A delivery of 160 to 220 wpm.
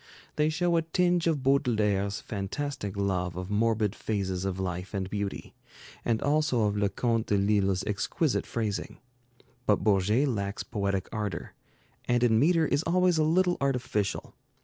No: average, 150 wpm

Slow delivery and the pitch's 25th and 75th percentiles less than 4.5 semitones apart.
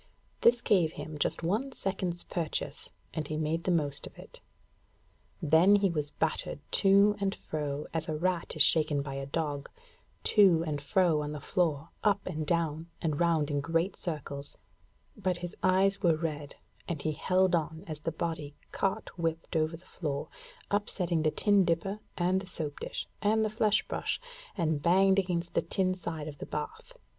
No: average, 180 wpm; average, 3.5 semitones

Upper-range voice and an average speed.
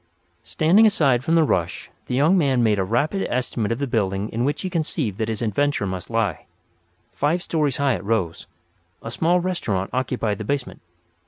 No: low, 125 Hz; average, 185 wpm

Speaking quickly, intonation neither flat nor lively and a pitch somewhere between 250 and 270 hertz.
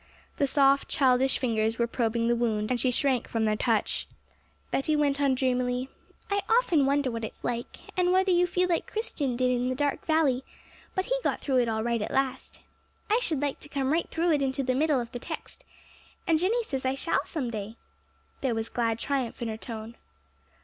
Yes: fast, 210 wpm; average, 4.0 semitones; very high, 260 Hz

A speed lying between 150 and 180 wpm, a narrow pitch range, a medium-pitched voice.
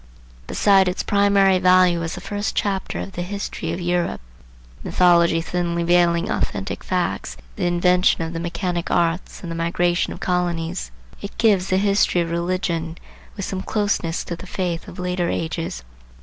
Yes: average, 165 wpm; narrow, 1.8 semitones; medium, 175 Hz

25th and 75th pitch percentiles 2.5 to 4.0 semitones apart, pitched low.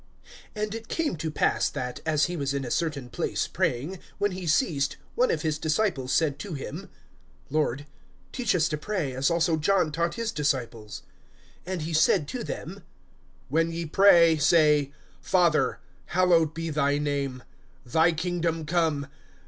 No: average, 3.6 semitones; medium, 160 Hz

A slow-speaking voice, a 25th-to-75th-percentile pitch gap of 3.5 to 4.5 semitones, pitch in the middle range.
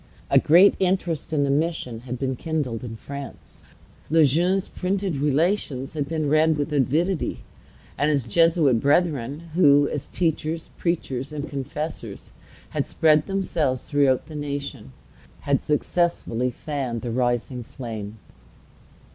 Yes: slow, 130 wpm; average, 3.9 semitones; medium, 145 Hz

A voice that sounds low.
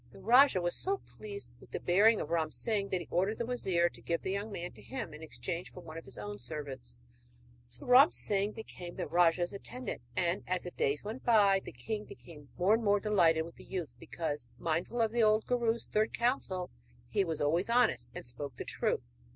No: medium, 185 Hz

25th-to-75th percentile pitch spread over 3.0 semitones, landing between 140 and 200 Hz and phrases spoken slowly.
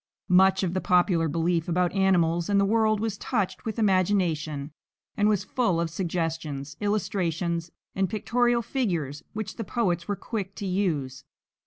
No: average, 3.7 semitones; medium, 185 Hz; average, 155 wpm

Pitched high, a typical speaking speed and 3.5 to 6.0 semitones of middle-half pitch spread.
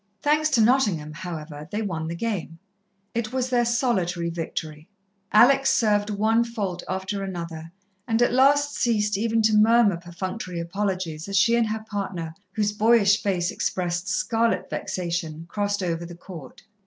Yes: high, 200 Hz; average, 155 wpm; average, 4.8 semitones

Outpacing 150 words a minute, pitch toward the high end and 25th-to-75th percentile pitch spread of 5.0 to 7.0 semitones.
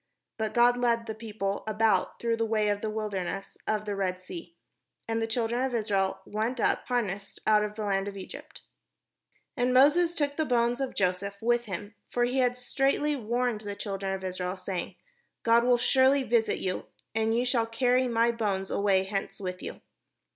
No: average, 190 wpm; high, 220 Hz; average, 3.6 semitones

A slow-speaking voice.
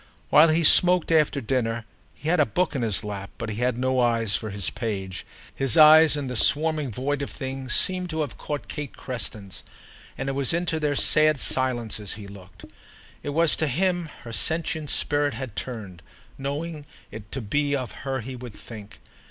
No: average, 190 wpm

